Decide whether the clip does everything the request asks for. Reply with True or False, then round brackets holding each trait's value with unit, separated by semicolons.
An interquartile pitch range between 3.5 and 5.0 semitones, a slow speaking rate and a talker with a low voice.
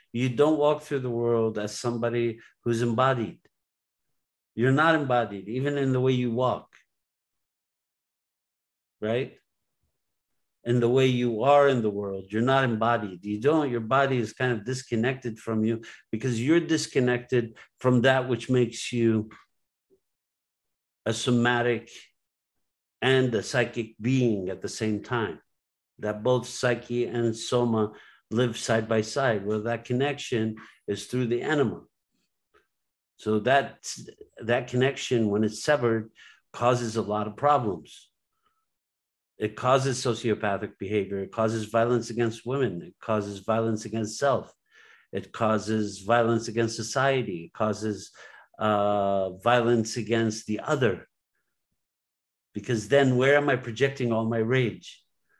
False (2.8 semitones; 130 wpm; 115 Hz)